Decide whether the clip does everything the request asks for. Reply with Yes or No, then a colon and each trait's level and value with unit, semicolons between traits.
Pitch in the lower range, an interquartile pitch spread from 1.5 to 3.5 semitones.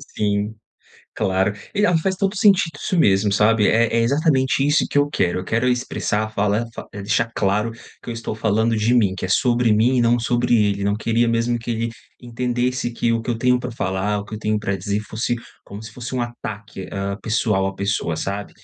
Yes: low, 115 Hz; average, 3.0 semitones